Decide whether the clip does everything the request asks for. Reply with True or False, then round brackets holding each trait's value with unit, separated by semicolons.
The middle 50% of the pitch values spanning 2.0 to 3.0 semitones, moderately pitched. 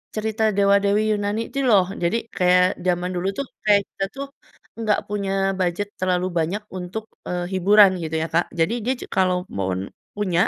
False (2.7 semitones; 195 Hz)